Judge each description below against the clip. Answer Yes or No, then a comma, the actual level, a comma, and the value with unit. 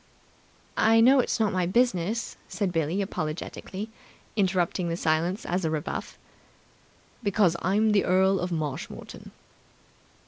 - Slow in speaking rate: Yes, slow, 125 wpm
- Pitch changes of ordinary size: Yes, average, 3.6 semitones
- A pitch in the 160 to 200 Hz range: Yes, medium, 185 Hz